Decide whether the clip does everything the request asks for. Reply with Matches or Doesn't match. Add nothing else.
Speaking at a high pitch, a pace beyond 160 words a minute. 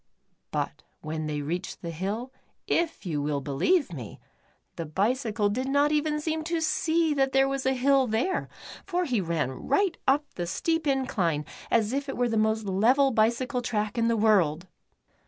Matches